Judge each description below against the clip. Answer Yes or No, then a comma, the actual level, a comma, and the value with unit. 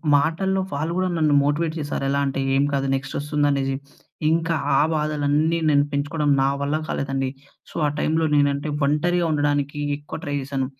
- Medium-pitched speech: Yes, medium, 145 Hz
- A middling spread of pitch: No, narrow, 1.9 semitones